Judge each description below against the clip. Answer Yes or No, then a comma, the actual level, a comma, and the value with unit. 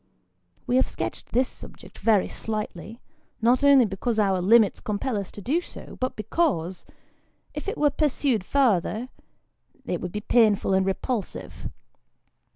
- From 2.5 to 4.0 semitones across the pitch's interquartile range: No, average, 4.7 semitones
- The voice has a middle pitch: No, high, 225 Hz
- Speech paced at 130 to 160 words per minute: Yes, average, 145 wpm